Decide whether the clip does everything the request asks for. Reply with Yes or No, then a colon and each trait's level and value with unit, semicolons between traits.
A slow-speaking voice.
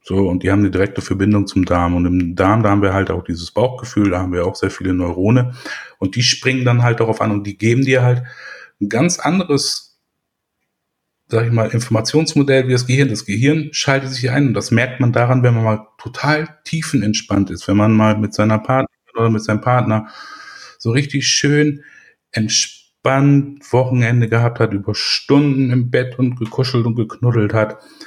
No: fast, 190 wpm